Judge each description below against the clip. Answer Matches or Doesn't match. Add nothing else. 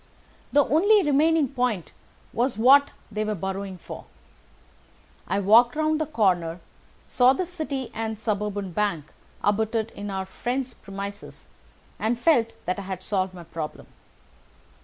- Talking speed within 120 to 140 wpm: Matches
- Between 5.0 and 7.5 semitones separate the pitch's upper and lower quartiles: Matches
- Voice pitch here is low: Doesn't match